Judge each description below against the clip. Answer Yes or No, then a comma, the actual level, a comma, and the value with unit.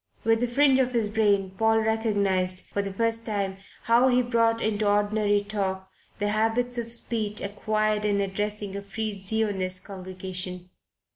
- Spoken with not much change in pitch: Yes, narrow, 2.3 semitones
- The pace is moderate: Yes, average, 155 wpm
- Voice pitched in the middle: No, high, 210 Hz